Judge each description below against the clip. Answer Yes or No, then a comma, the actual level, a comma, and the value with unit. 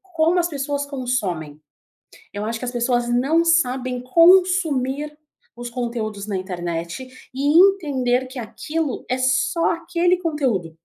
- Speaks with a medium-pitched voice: No, very high, 255 Hz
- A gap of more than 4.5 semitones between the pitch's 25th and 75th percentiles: Yes, average, 5.1 semitones